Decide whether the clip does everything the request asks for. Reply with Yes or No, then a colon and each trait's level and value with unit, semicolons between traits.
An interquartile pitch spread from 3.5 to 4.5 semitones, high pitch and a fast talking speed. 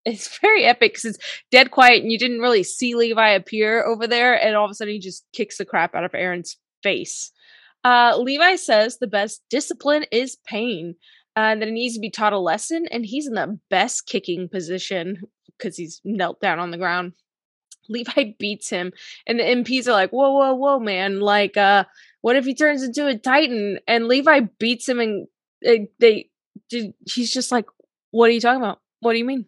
Yes: average, 4.0 semitones; high, 230 Hz; fast, 210 wpm